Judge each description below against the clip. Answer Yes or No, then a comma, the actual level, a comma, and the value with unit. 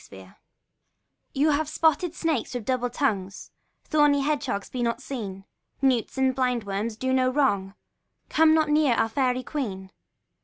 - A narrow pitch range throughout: No, average, 4.7 semitones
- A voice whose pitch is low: No, very high, 255 Hz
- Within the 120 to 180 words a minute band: Yes, average, 160 wpm